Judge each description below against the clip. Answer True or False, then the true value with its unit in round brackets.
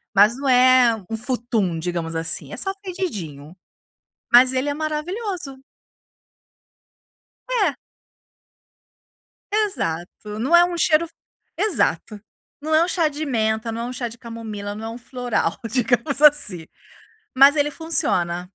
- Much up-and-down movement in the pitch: True (6.6 semitones)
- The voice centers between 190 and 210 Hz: False (250 Hz)